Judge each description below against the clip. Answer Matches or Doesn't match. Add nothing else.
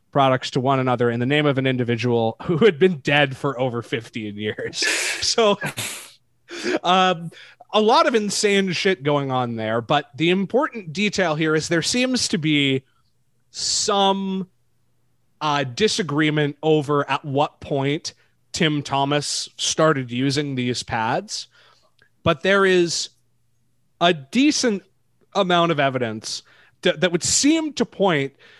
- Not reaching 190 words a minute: Matches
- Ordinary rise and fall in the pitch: Doesn't match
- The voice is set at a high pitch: Doesn't match